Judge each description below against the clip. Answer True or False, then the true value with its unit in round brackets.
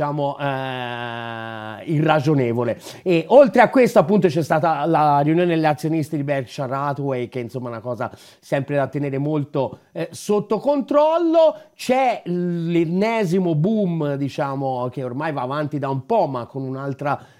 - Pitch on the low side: False (150 Hz)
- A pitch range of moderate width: True (4.9 semitones)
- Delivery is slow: False (145 wpm)